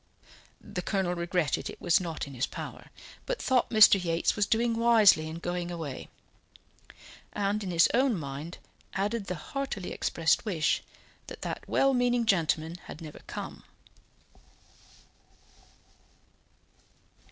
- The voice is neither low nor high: Yes, medium, 180 Hz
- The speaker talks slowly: Yes, slow, 130 wpm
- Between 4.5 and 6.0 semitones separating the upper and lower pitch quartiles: Yes, average, 5.1 semitones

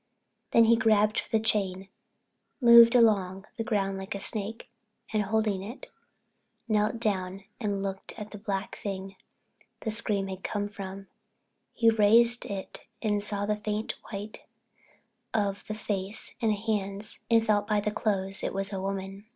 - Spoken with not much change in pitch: Yes, narrow, 2.0 semitones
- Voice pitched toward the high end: Yes, high, 205 Hz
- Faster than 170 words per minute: No, average, 160 wpm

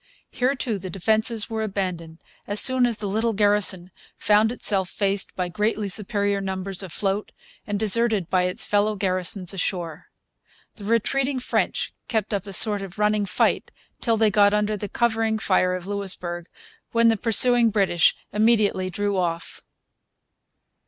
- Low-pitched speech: No, high, 205 Hz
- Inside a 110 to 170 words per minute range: Yes, average, 150 wpm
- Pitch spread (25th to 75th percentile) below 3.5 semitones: Yes, average, 2.7 semitones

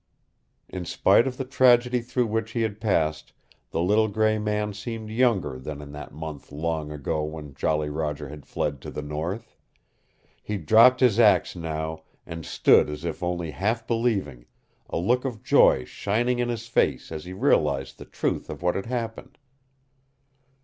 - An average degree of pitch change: No, wide, 6.9 semitones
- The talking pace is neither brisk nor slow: Yes, average, 170 wpm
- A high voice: No, very low, 95 Hz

